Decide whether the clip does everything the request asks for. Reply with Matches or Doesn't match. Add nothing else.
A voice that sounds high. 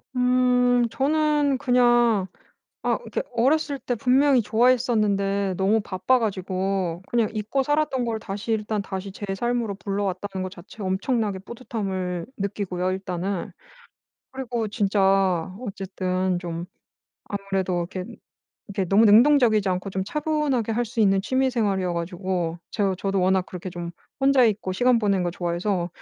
Matches